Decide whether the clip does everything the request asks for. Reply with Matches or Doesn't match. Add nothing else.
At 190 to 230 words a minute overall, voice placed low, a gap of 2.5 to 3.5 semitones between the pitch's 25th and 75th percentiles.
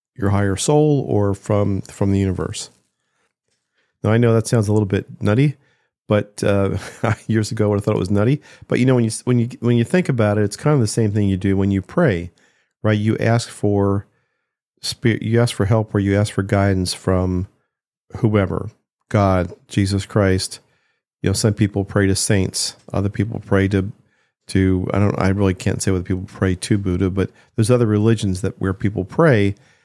Matches